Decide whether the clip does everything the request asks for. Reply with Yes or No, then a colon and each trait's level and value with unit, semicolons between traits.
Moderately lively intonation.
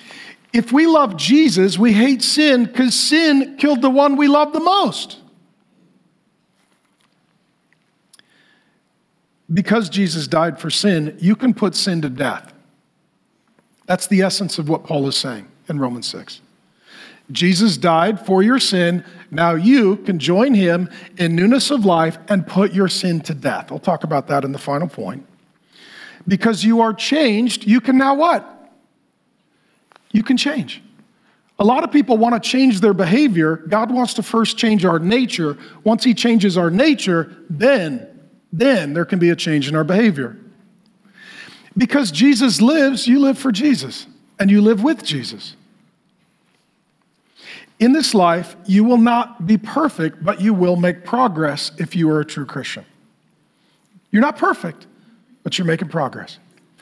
No: wide, 6.5 semitones